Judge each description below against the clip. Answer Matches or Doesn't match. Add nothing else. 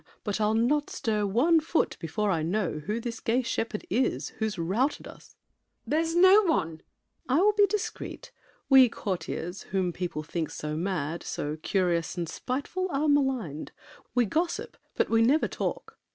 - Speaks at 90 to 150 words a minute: Doesn't match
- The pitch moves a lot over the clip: Matches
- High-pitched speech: Matches